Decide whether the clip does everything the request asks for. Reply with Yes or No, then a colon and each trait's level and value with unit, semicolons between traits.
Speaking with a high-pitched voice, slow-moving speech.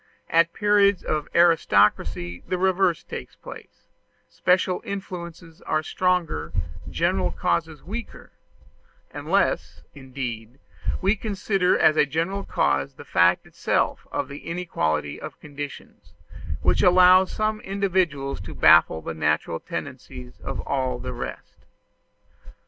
No: medium, 165 Hz; slow, 115 wpm